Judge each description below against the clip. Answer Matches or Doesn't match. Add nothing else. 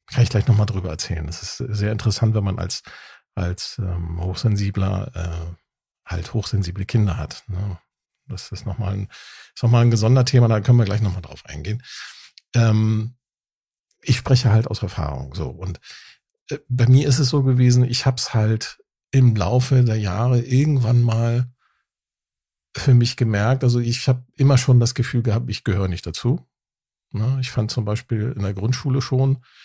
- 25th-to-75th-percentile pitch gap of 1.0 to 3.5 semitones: Doesn't match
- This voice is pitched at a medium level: Doesn't match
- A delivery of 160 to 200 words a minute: Matches